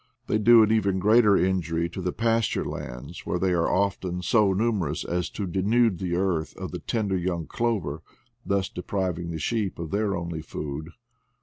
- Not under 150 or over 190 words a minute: Yes, average, 175 wpm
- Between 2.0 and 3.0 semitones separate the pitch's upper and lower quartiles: No, average, 3.7 semitones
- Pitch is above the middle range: No, very low, 95 Hz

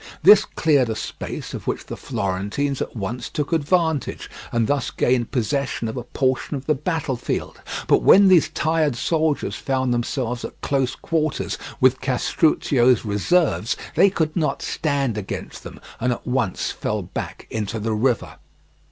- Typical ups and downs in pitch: Yes, average, 4.5 semitones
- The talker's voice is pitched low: Yes, low, 130 Hz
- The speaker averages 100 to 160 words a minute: Yes, average, 155 wpm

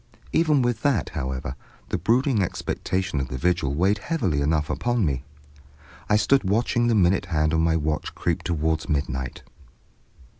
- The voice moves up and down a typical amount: No, wide, 6.8 semitones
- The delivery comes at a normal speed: Yes, average, 155 wpm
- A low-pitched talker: Yes, very low, 85 Hz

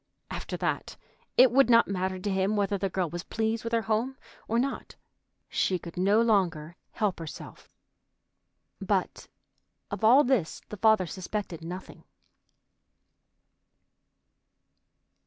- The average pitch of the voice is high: Yes, high, 200 Hz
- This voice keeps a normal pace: No, slow, 125 wpm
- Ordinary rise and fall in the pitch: Yes, average, 3.8 semitones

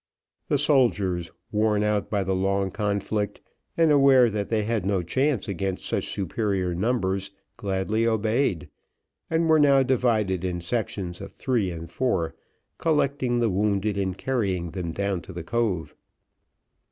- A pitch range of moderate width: Yes, average, 4.3 semitones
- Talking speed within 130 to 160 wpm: Yes, average, 145 wpm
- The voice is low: Yes, low, 105 Hz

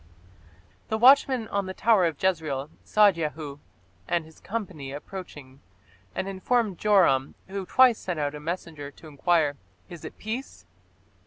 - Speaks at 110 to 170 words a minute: Yes, average, 145 wpm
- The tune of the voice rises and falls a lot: Yes, wide, 5.8 semitones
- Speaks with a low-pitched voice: No, medium, 175 Hz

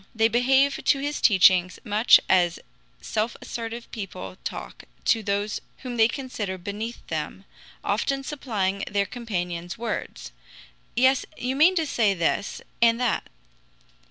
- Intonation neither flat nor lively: Yes, average, 4.2 semitones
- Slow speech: Yes, slow, 130 wpm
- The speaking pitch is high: Yes, high, 225 Hz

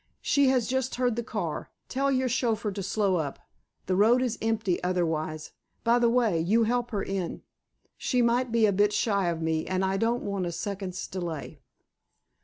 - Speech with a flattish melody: No, average, 4.7 semitones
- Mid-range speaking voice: No, high, 210 Hz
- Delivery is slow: No, average, 190 wpm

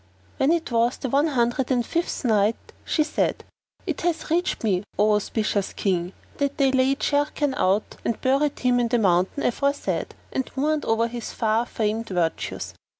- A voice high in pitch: Yes, high, 245 Hz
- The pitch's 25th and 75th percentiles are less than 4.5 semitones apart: No, average, 4.8 semitones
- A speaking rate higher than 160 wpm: Yes, average, 170 wpm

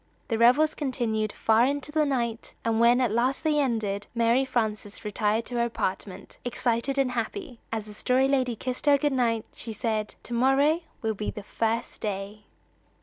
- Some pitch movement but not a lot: Yes, average, 3.2 semitones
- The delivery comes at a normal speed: Yes, average, 180 wpm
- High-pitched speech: Yes, high, 235 Hz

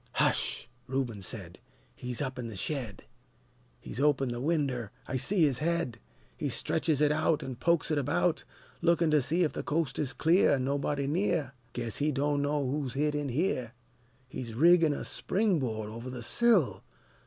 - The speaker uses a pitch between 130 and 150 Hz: Yes, medium, 140 Hz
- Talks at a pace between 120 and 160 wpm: No, average, 175 wpm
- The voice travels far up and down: No, average, 4.1 semitones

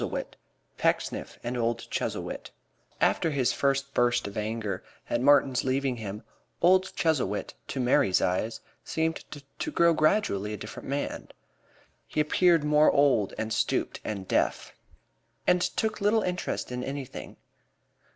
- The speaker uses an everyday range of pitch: No, wide, 5.9 semitones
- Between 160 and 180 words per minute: No, slow, 135 wpm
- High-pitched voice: No, low, 135 Hz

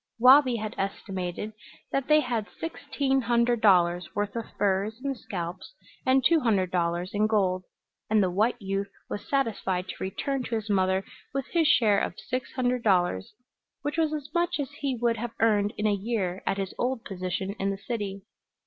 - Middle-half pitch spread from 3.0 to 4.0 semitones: No, average, 4.7 semitones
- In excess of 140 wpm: Yes, average, 185 wpm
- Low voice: No, high, 215 Hz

